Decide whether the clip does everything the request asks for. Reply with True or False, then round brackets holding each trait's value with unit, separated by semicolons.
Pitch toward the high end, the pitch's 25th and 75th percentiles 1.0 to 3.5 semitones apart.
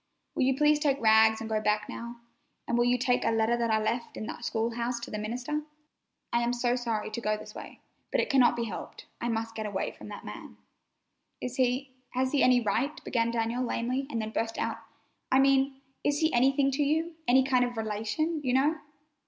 True (245 Hz; 3.0 semitones)